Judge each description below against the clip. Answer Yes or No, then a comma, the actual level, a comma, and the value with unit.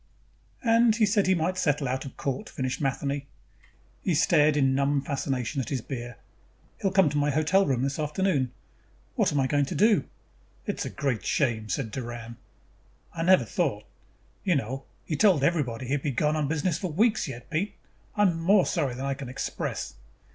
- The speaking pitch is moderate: Yes, medium, 145 Hz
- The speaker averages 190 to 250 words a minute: Yes, average, 200 wpm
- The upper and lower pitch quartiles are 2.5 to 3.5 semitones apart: No, average, 4.7 semitones